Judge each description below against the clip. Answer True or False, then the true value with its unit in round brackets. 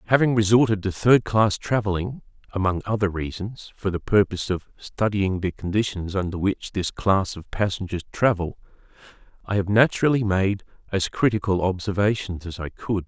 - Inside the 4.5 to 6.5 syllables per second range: True (5.2 syllables/s)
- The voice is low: True (100 Hz)